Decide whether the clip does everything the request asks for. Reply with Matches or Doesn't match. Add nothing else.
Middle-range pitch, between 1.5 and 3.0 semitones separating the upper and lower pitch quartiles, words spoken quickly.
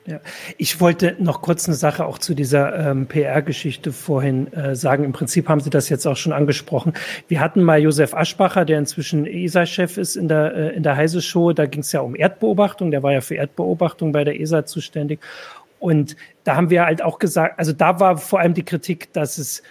Matches